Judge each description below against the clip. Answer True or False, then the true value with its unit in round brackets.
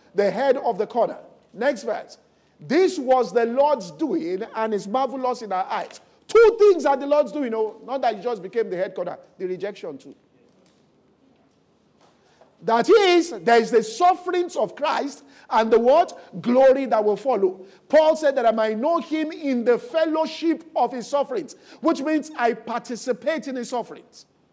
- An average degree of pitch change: False (5.7 semitones)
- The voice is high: True (255 Hz)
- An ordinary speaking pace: True (175 wpm)